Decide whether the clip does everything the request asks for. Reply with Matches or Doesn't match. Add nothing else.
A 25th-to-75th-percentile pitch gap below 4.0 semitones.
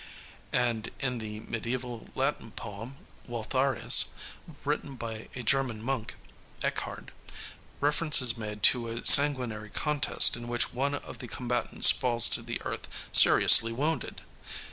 Matches